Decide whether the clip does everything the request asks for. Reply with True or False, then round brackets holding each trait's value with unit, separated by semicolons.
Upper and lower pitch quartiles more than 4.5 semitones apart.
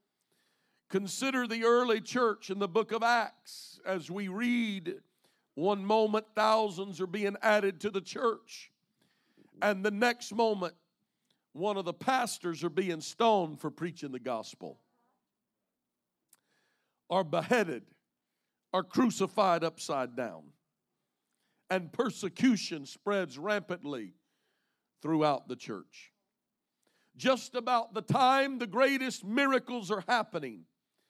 True (4.9 semitones)